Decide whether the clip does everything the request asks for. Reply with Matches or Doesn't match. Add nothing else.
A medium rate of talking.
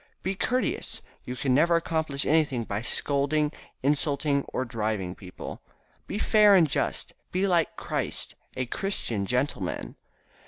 Doesn't match